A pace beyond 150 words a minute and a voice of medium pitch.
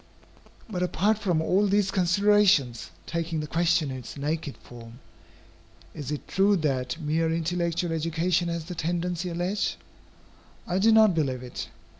No: average, 145 wpm; medium, 170 Hz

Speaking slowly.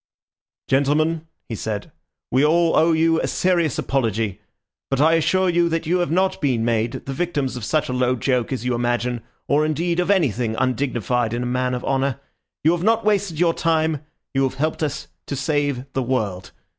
No: average, 190 wpm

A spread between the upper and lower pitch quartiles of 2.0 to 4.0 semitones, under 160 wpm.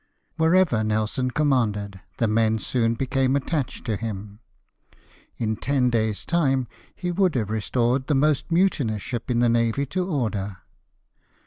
No: average, 4.5 semitones; average, 145 wpm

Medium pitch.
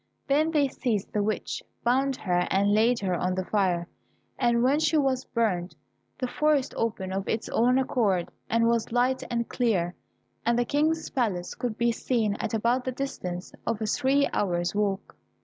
No: high, 230 Hz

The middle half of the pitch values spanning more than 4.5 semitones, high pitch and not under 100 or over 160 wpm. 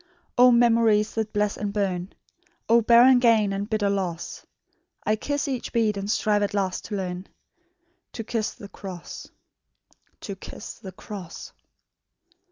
No: average, 2.7 semitones; high, 210 Hz; average, 145 wpm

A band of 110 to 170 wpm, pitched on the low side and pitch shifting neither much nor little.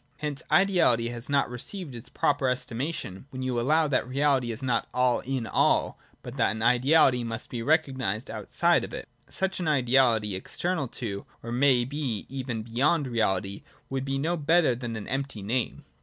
No: average, 185 wpm; low, 130 Hz; average, 3.4 semitones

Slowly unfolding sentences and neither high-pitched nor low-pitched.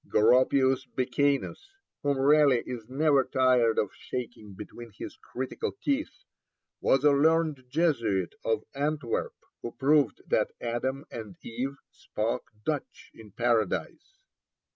No: slow, 120 wpm; low, 130 Hz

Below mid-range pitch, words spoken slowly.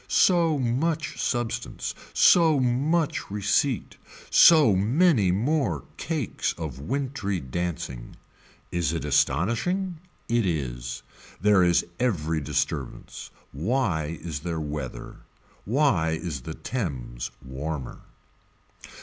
Yes: very low, 95 Hz; slow, 100 wpm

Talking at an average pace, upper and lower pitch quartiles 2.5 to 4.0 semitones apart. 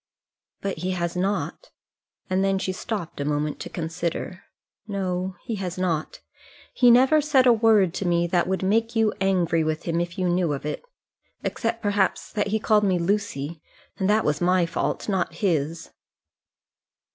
Yes: average, 170 wpm; average, 3.5 semitones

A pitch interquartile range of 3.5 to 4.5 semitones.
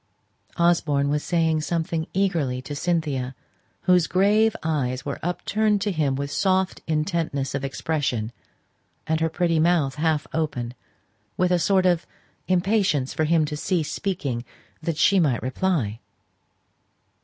Yes: average, 4.1 semitones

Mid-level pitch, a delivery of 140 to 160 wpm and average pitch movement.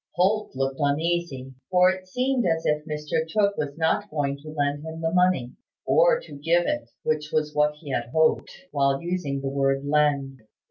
No: medium, 150 Hz; average, 185 wpm; average, 3.7 semitones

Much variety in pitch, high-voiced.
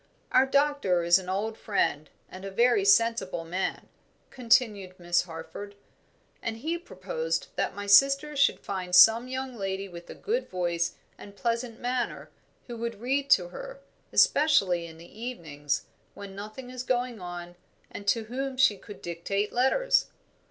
Yes: wide, 5.7 semitones; high, 215 Hz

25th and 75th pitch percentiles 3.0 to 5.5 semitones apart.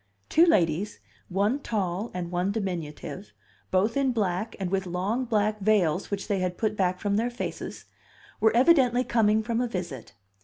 Yes: average, 4.0 semitones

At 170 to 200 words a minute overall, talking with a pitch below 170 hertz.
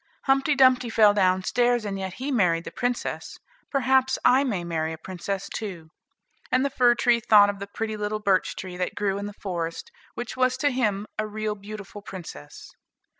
No: average, 190 wpm; high, 210 Hz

